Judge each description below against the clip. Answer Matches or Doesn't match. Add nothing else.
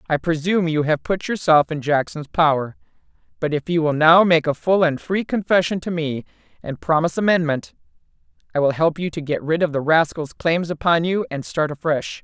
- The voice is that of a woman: Matches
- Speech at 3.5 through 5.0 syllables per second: Doesn't match